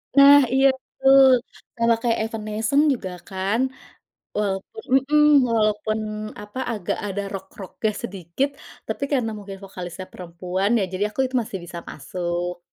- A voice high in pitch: Yes, high, 210 Hz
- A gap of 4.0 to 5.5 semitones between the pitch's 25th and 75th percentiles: Yes, average, 4.5 semitones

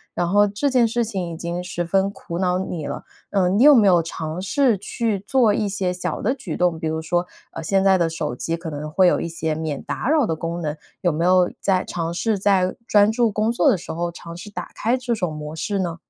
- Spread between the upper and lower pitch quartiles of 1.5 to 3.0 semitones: No, average, 3.8 semitones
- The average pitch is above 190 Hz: No, medium, 185 Hz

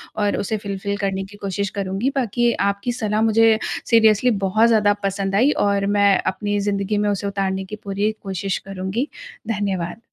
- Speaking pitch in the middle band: No, high, 200 Hz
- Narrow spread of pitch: Yes, narrow, 1.8 semitones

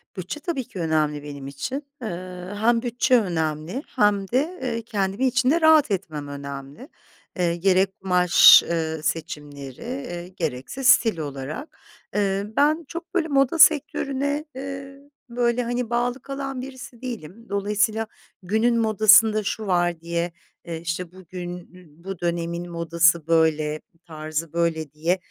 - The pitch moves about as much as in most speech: No, wide, 6.8 semitones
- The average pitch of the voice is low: No, high, 190 Hz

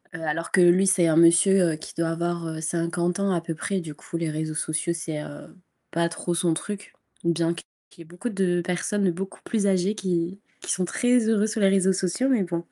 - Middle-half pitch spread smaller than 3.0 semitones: Yes, narrow, 2.6 semitones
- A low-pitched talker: No, medium, 175 Hz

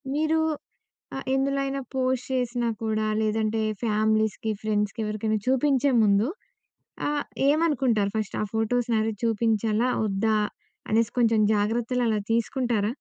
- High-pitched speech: Yes, high, 225 Hz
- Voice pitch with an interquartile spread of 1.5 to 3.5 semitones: Yes, average, 2.8 semitones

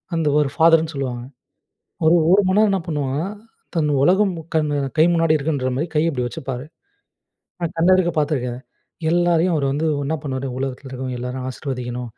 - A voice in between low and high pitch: Yes, medium, 150 Hz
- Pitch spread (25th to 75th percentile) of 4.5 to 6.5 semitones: No, average, 4.1 semitones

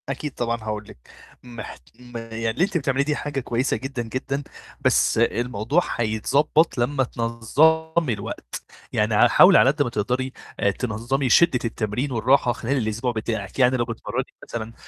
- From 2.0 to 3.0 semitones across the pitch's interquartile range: No, average, 3.4 semitones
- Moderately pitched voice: No, low, 120 Hz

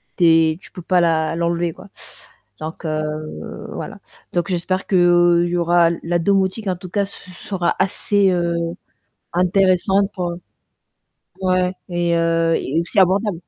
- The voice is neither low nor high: Yes, medium, 175 Hz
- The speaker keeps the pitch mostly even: Yes, narrow, 2.0 semitones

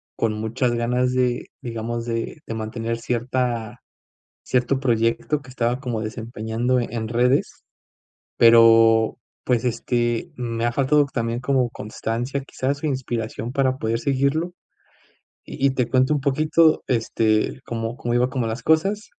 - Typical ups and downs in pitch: No, narrow, 2.3 semitones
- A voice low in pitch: Yes, low, 120 Hz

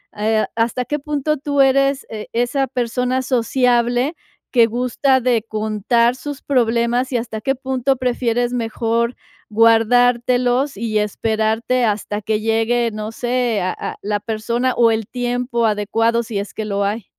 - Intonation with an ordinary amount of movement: No, narrow, 2.3 semitones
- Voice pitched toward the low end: No, high, 235 Hz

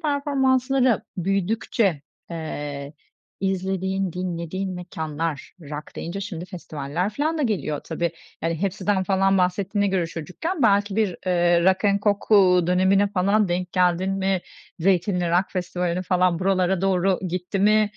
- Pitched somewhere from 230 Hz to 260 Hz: No, medium, 185 Hz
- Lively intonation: No, narrow, 2.4 semitones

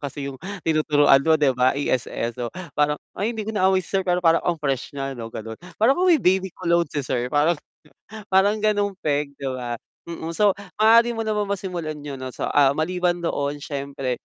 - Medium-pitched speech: Yes, medium, 155 Hz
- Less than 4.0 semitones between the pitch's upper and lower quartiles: No, wide, 5.6 semitones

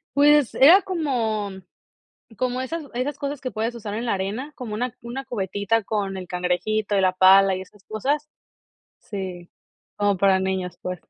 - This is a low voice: No, high, 215 Hz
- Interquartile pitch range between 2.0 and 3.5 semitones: No, average, 5.1 semitones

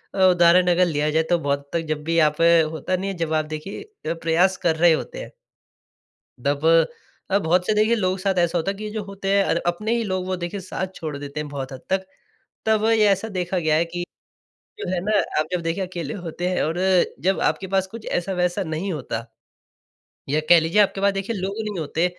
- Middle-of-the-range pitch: Yes, medium, 180 Hz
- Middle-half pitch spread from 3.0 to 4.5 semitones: Yes, average, 3.4 semitones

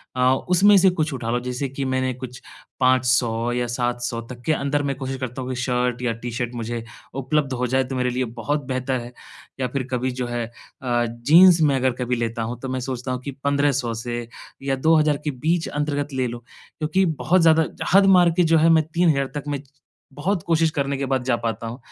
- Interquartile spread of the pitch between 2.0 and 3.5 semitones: Yes, average, 3.1 semitones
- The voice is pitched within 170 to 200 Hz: No, low, 130 Hz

